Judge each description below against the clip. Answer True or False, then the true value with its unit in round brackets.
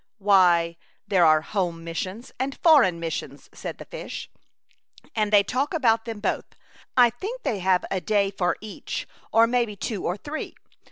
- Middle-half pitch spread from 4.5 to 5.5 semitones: True (4.9 semitones)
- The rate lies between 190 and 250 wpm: False (175 wpm)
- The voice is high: True (205 Hz)